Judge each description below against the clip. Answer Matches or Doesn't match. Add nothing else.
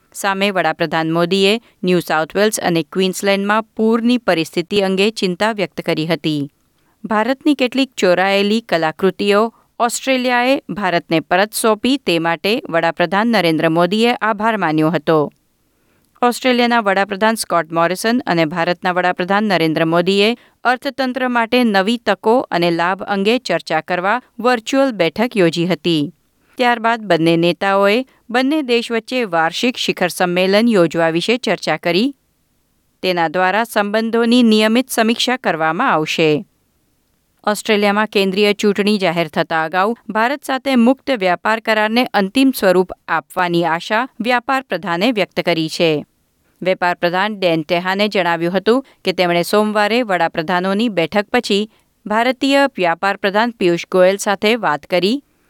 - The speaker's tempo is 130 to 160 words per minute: Doesn't match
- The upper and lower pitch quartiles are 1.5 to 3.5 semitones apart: Doesn't match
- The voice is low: Doesn't match